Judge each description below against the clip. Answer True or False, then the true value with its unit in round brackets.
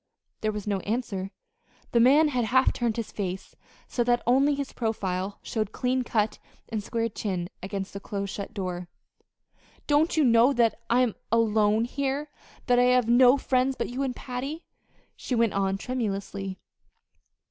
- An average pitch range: True (4.0 semitones)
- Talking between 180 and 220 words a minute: False (165 wpm)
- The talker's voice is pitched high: True (230 Hz)